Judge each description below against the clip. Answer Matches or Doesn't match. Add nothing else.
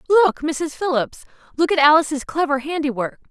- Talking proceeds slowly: Matches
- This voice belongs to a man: Doesn't match